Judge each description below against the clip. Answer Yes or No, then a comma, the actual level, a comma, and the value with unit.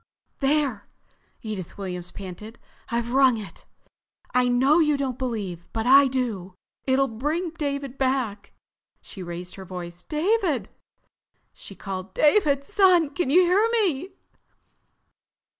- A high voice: Yes, very high, 260 Hz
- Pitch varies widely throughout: Yes, wide, 7.0 semitones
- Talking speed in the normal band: No, slow, 125 wpm